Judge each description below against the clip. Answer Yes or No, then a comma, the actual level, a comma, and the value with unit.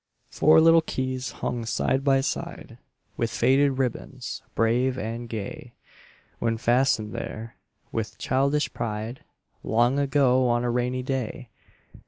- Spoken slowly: Yes, slow, 125 wpm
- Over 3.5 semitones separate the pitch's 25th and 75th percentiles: No, narrow, 2.6 semitones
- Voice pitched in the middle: No, low, 125 Hz